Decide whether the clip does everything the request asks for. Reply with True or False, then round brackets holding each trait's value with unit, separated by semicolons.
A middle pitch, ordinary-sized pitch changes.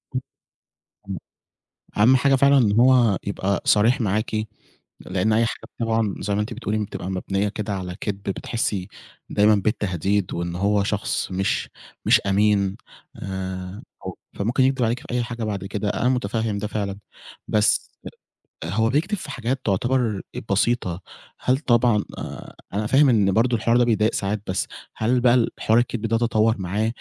False (110 Hz; 3.2 semitones)